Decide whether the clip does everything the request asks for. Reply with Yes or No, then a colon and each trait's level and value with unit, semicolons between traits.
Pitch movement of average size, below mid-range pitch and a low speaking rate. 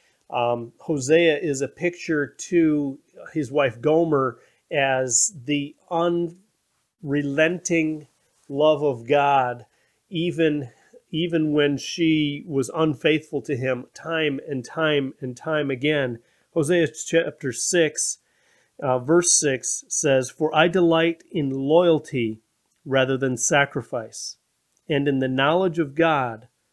No: average, 3.3 semitones; medium, 150 Hz; slow, 110 wpm